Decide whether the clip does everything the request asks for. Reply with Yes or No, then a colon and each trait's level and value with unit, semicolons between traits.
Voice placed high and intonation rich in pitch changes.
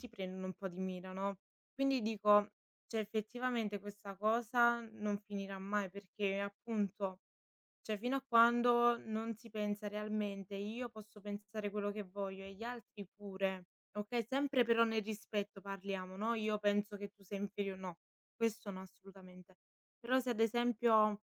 No: high, 210 Hz; narrow, 2.4 semitones